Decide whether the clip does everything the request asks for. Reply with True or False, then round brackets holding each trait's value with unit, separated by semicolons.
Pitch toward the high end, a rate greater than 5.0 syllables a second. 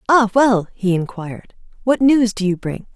False (215 Hz; 4.7 syllables/s)